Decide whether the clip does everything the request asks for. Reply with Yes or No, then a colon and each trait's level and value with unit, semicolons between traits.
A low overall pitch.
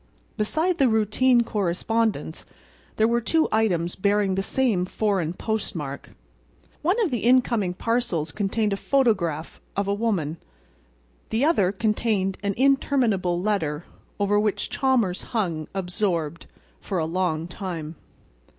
No: high, 205 Hz